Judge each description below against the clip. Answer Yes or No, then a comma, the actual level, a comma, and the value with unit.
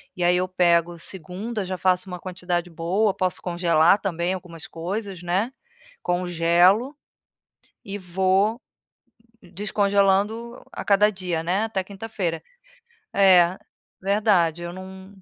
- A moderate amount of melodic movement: No, narrow, 2.3 semitones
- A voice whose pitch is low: No, medium, 185 Hz